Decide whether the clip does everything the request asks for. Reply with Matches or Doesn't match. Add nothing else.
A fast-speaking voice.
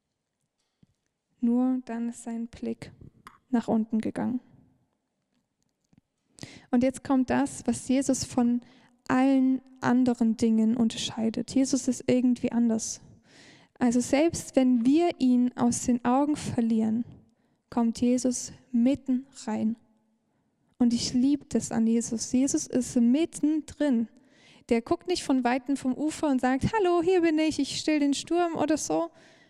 Doesn't match